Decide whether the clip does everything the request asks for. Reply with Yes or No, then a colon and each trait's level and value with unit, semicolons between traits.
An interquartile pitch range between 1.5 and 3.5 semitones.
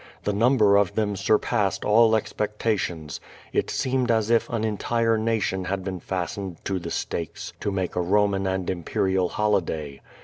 Yes: average, 2.9 semitones